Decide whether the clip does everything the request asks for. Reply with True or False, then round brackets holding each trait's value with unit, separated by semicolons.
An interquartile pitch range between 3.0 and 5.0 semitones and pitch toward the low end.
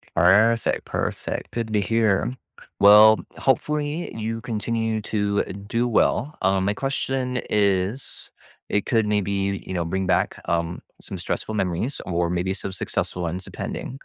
True (3.4 semitones; 105 Hz)